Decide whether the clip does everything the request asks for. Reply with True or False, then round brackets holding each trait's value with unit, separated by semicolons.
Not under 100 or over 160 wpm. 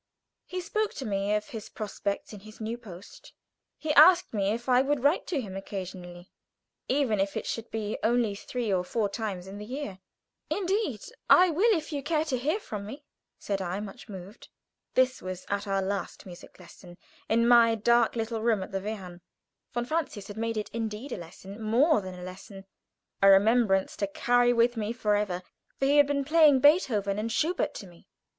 False (195 wpm)